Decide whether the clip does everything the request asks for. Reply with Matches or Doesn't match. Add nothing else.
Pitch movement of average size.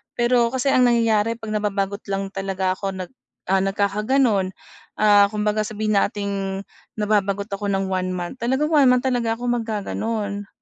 Matches